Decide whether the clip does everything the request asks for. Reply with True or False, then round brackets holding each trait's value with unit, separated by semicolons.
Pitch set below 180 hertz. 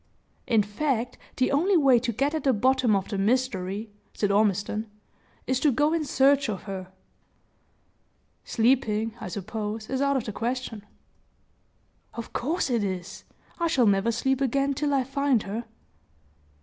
False (240 Hz)